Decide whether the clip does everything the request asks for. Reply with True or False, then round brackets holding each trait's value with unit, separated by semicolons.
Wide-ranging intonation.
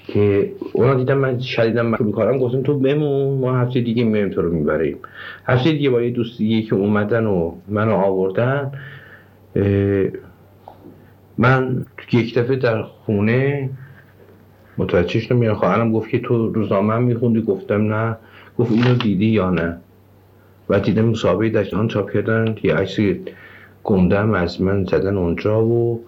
False (3.4 semitones)